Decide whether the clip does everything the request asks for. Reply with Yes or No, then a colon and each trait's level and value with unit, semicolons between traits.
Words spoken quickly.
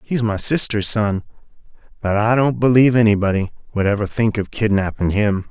No: average, 165 wpm